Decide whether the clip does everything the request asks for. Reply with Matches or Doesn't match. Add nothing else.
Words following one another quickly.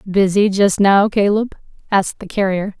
Doesn't match